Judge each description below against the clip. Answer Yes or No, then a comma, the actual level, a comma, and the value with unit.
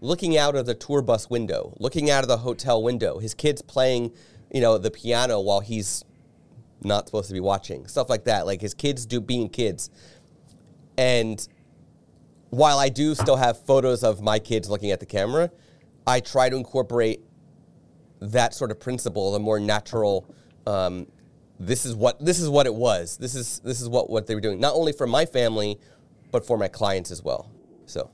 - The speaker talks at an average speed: Yes, average, 195 wpm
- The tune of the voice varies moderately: Yes, average, 3.5 semitones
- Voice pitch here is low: Yes, low, 120 Hz